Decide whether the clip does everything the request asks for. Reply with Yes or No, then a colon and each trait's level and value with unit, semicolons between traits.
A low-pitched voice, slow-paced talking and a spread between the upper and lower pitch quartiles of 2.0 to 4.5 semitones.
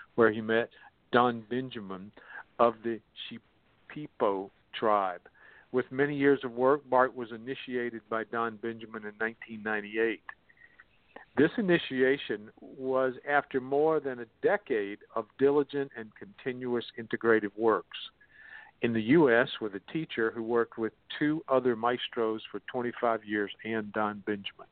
Yes: low, 115 Hz; slow, 130 wpm; average, 2.8 semitones